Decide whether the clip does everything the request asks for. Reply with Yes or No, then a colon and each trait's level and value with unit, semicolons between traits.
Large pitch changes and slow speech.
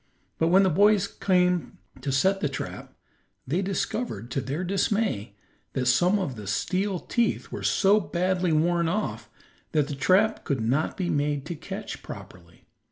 No: wide, 5.7 semitones; average, 165 wpm